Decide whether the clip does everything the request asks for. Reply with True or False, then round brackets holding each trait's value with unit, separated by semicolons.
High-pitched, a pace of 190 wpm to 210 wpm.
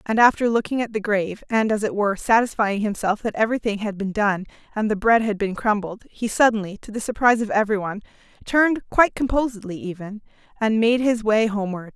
True (215 Hz; 200 wpm)